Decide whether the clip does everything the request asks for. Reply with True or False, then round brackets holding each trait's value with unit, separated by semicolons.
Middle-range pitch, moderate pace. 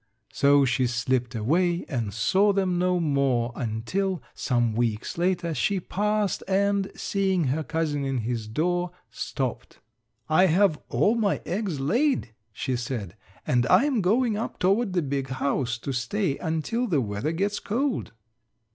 True (160 Hz; 145 wpm)